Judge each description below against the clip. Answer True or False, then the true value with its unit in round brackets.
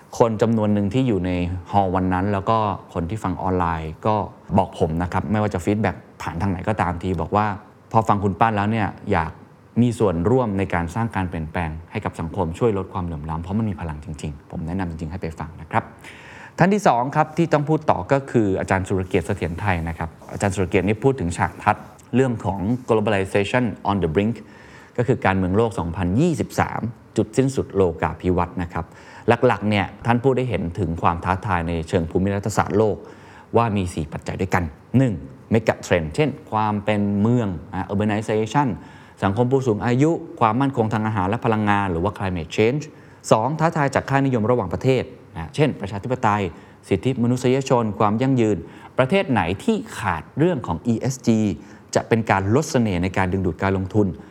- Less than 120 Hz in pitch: True (105 Hz)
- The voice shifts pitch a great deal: False (4.3 semitones)